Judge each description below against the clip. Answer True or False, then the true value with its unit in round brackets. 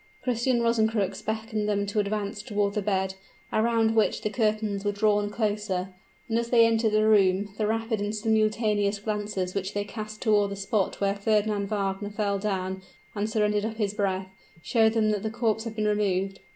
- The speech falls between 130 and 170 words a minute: False (185 wpm)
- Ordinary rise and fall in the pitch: False (1.6 semitones)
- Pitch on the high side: True (210 Hz)